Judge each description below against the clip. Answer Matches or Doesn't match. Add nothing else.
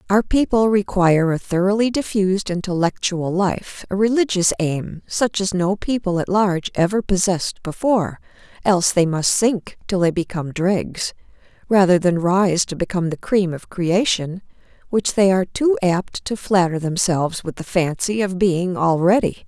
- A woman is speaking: Matches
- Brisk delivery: Doesn't match